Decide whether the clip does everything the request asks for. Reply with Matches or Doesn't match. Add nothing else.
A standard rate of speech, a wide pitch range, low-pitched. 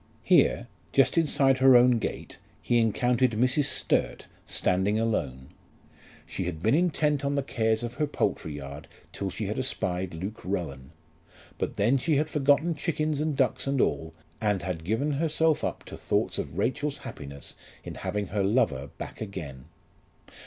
Matches